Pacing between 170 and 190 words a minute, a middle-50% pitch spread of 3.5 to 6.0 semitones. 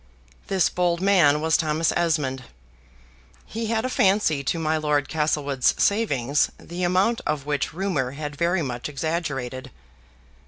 No: slow, 135 wpm; average, 4.1 semitones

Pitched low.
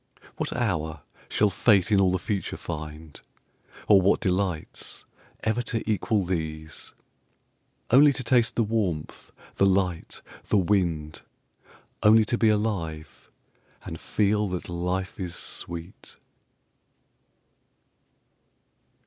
Yes: very low, 95 Hz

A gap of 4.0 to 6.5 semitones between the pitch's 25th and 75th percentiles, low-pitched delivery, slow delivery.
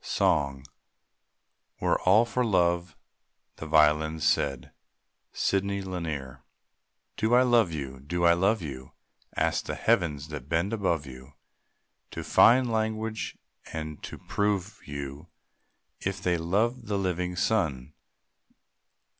Yes: wide, 5.6 semitones; very low, 85 Hz; slow, 120 wpm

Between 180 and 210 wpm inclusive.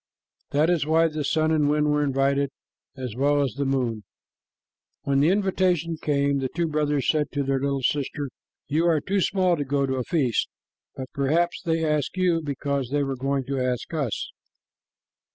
Yes: average, 185 wpm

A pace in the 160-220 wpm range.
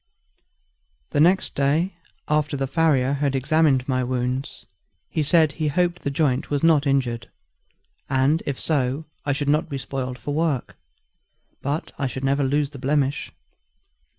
No: average, 150 wpm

